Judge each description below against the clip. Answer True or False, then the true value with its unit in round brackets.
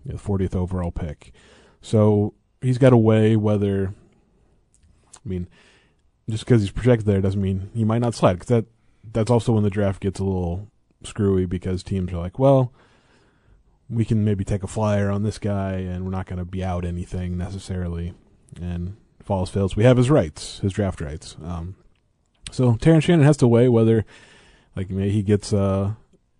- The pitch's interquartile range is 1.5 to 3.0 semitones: False (3.4 semitones)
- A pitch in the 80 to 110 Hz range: True (100 Hz)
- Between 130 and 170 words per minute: False (180 wpm)